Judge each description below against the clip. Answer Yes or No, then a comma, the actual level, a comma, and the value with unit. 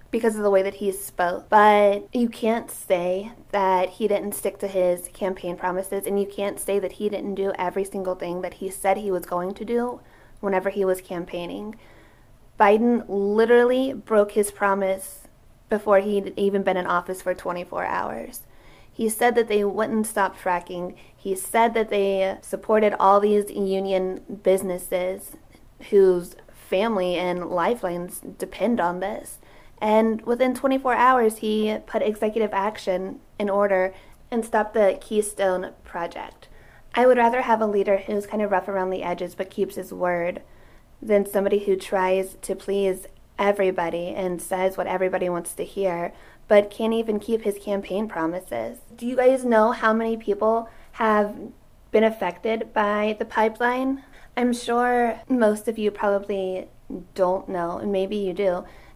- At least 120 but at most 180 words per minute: Yes, average, 160 wpm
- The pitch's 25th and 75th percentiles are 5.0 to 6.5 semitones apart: No, average, 2.7 semitones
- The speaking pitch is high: Yes, high, 200 Hz